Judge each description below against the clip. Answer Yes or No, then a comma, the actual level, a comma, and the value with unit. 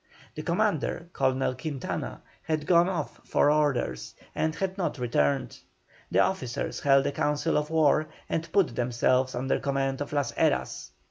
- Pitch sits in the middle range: Yes, medium, 145 Hz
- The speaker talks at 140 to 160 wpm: Yes, average, 150 wpm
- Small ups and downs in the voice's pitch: No, average, 3.7 semitones